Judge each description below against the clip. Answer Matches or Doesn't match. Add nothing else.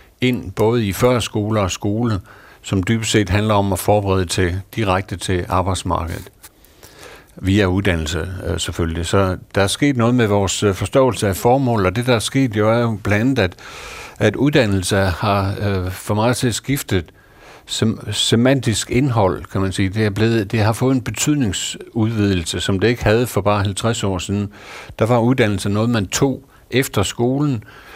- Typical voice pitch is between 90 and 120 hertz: Matches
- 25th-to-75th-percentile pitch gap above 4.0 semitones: Doesn't match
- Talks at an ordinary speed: Matches